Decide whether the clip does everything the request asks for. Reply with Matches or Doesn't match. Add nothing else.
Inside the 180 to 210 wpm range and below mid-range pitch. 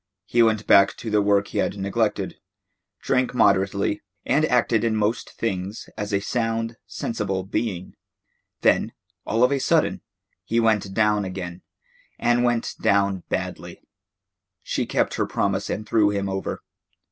Doesn't match